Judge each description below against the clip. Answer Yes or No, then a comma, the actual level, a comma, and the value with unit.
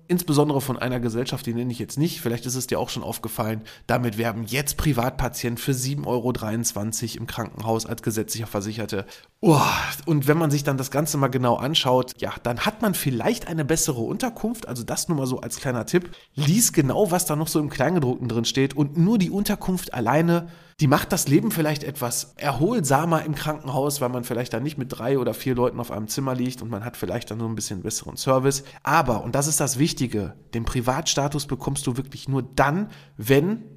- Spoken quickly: Yes, fast, 210 wpm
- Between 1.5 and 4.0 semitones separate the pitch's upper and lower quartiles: No, average, 4.4 semitones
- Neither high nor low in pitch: No, low, 130 Hz